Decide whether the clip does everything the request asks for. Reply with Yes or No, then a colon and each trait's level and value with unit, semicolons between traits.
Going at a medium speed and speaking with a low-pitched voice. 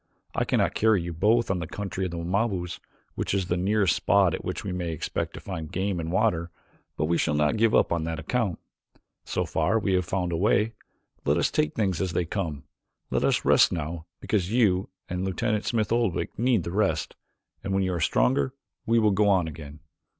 No: fast, 215 wpm; very low, 95 Hz